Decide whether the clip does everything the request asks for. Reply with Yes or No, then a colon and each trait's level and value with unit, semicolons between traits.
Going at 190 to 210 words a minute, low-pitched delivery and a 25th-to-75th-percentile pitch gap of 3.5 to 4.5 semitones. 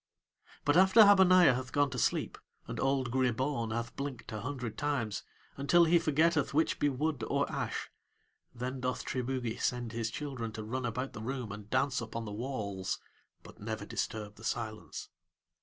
No: average, 170 wpm; low, 130 Hz; average, 4.0 semitones